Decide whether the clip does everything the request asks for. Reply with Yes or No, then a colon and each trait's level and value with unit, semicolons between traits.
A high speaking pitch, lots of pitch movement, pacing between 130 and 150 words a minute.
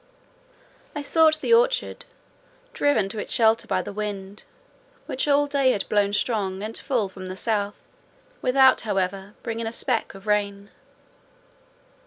No: high, 215 Hz; average, 4.9 semitones; average, 145 wpm